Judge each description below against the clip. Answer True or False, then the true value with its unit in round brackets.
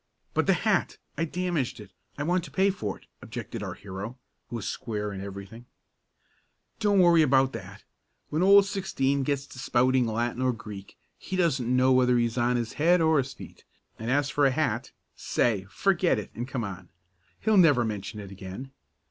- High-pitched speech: False (130 Hz)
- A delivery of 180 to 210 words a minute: True (190 wpm)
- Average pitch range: False (6.3 semitones)